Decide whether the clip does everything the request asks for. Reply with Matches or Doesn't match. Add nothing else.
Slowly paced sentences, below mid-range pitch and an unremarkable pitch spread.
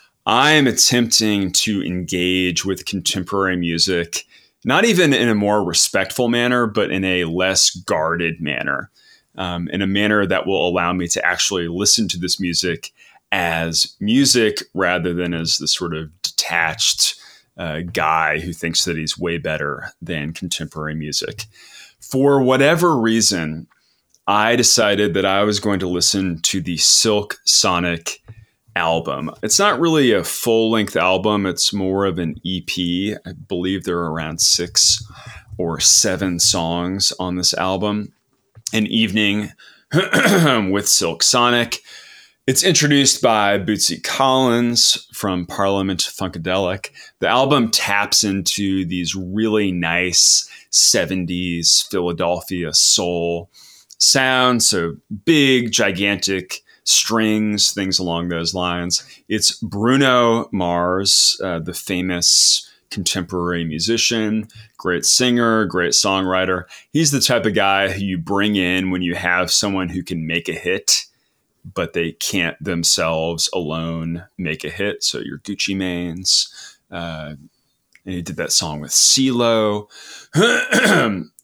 Matches